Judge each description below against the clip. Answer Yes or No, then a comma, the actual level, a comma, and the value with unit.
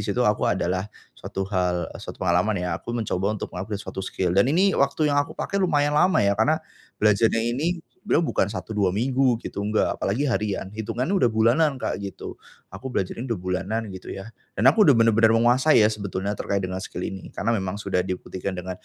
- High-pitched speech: No, low, 110 Hz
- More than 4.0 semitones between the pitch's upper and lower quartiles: Yes, average, 4.9 semitones